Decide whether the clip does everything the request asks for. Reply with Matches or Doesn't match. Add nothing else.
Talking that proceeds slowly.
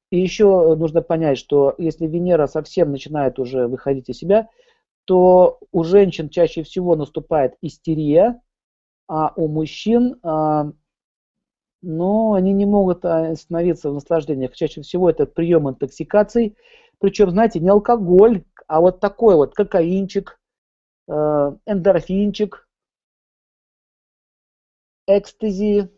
Matches